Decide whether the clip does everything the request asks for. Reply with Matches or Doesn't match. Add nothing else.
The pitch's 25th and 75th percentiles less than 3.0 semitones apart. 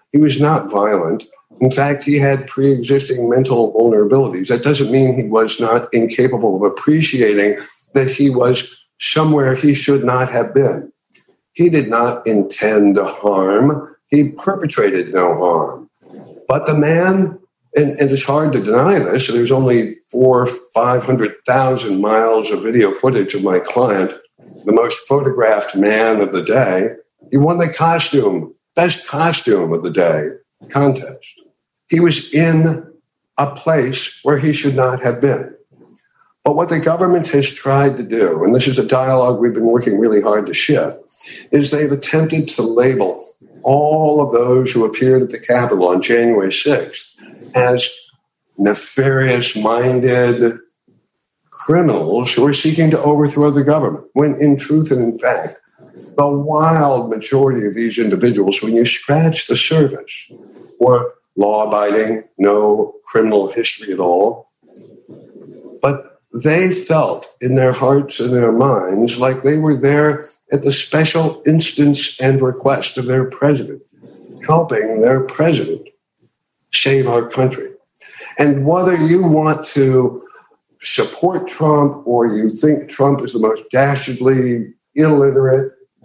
Doesn't match